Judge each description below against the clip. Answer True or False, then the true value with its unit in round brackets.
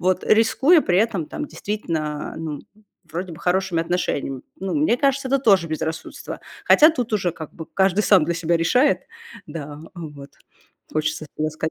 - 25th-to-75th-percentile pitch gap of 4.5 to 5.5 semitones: True (5.2 semitones)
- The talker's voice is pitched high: False (175 Hz)